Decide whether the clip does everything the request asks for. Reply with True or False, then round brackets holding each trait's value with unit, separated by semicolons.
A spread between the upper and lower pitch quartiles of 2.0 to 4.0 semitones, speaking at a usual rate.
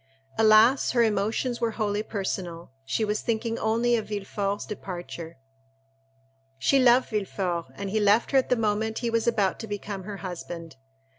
True (2.7 semitones; 160 wpm)